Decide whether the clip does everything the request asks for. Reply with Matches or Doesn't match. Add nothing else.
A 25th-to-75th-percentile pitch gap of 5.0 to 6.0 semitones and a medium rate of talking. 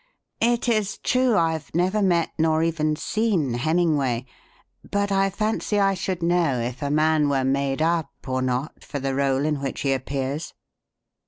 Matches